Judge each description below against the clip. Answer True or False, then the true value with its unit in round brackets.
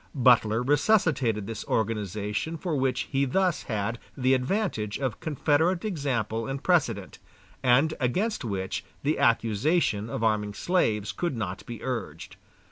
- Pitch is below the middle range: True (125 Hz)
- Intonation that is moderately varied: False (6.0 semitones)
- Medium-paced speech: False (130 wpm)